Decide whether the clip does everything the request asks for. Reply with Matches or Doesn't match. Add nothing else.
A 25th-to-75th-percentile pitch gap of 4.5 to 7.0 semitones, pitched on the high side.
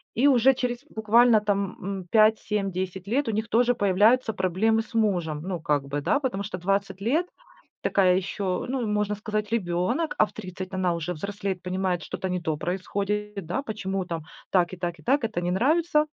Doesn't match